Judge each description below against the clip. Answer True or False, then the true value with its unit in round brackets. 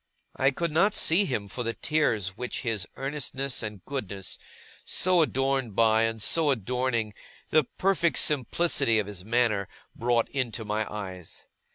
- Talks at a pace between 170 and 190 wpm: False (150 wpm)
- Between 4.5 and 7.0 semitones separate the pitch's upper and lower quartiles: True (4.8 semitones)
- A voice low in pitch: True (120 Hz)